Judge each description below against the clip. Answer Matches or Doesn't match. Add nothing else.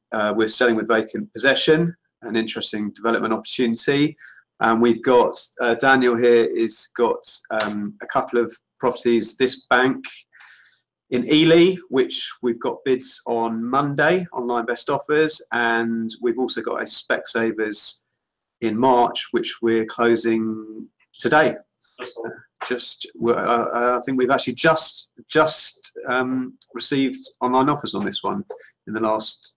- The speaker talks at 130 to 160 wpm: Matches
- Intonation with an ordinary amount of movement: Matches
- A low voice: Matches